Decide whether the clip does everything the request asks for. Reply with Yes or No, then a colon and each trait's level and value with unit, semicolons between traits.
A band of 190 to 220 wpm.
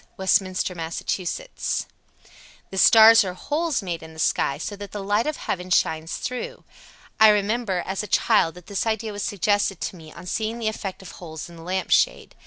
Yes: average, 195 wpm